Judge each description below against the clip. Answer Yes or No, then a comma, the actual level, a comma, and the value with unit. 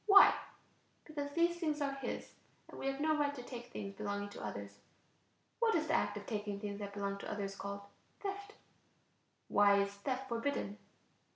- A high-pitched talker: Yes, high, 230 Hz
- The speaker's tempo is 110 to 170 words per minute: No, average, 180 wpm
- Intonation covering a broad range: Yes, wide, 6.3 semitones